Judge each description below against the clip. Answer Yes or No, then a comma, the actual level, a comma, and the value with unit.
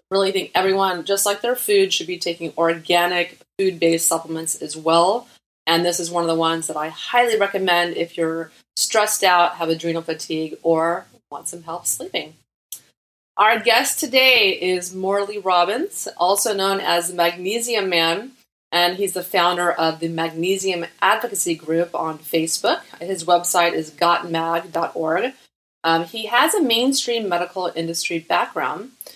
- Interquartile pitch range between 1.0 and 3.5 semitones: Yes, average, 2.8 semitones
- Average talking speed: Yes, average, 150 wpm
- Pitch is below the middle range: No, medium, 175 Hz